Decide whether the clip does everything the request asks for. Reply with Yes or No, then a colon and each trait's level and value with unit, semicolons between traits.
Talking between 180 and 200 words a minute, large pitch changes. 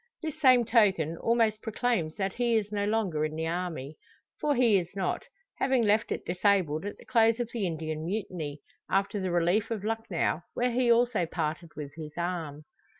Yes: average, 185 wpm; wide, 5.7 semitones